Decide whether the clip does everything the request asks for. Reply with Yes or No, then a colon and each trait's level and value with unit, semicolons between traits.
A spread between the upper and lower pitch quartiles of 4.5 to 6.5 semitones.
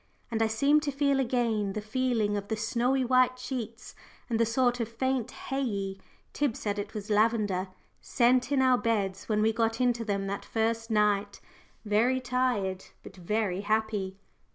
No: average, 3.3 semitones